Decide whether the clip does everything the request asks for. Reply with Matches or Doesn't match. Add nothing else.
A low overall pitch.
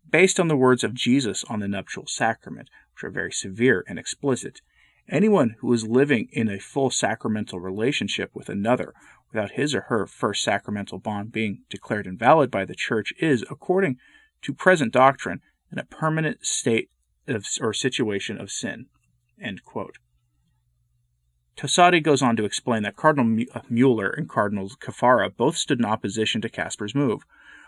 Matches